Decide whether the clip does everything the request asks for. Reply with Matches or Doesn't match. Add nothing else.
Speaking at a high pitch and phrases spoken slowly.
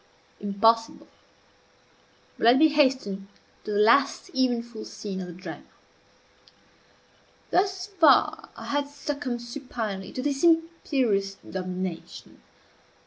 Matches